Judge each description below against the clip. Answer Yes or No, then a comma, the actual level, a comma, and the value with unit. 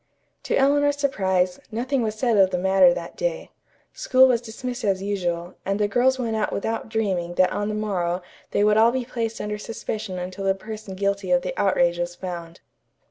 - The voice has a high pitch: Yes, high, 205 Hz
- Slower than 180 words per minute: No, average, 195 wpm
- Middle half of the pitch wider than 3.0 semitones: Yes, average, 3.8 semitones